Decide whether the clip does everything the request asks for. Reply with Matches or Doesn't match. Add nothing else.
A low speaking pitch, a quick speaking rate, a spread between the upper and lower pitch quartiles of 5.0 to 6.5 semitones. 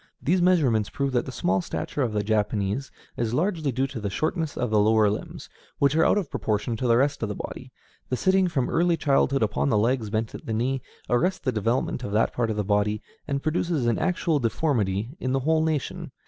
Matches